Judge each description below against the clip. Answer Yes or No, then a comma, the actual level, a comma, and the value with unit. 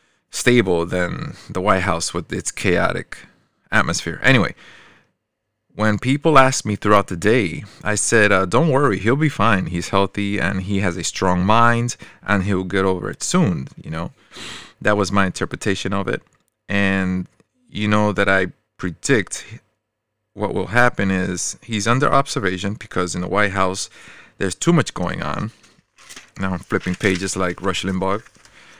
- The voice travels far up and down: No, narrow, 2.5 semitones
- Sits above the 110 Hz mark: No, low, 100 Hz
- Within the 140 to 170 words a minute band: Yes, average, 160 wpm